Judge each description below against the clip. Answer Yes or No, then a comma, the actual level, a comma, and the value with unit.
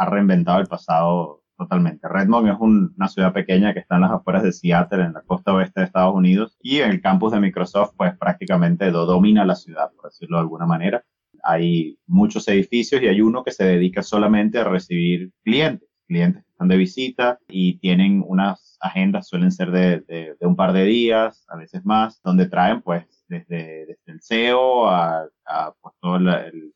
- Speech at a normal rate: No, fast, 200 wpm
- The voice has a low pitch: Yes, very low, 95 Hz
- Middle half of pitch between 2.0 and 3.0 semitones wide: No, average, 4.2 semitones